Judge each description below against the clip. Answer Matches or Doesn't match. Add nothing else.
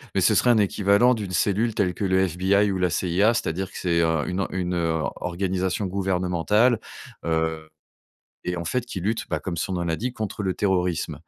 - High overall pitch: Doesn't match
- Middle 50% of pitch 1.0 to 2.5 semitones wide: Doesn't match